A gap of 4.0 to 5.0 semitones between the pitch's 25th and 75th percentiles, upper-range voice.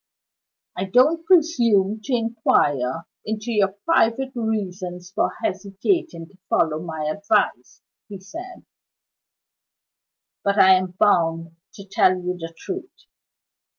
Yes: average, 4.6 semitones; high, 200 Hz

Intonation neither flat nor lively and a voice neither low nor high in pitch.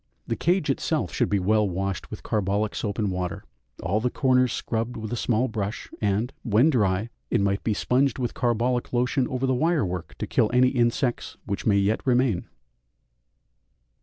No: average, 3.9 semitones; low, 115 Hz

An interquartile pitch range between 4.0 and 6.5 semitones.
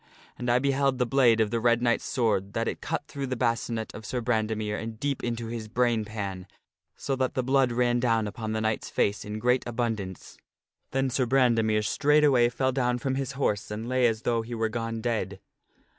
No: narrow, 2.6 semitones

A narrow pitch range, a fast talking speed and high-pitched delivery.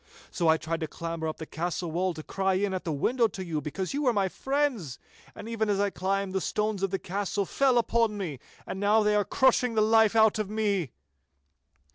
No: average, 3.9 semitones; fast, 225 wpm; high, 195 Hz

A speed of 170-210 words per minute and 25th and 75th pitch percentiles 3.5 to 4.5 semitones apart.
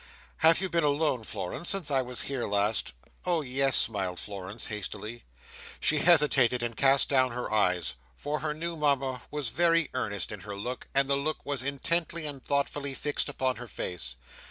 No: average, 180 wpm; average, 5.2 semitones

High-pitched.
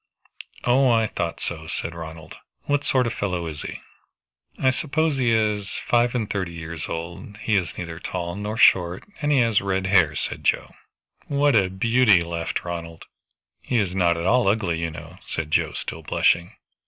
No: very low, 95 Hz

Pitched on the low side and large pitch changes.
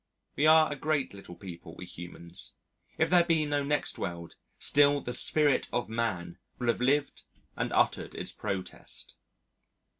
Yes: low, 125 Hz; wide, 8.6 semitones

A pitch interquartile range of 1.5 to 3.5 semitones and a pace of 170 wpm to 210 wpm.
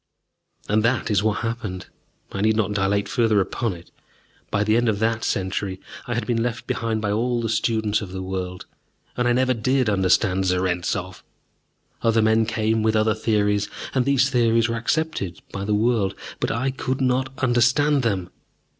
Yes: average, 3.1 semitones; average, 180 wpm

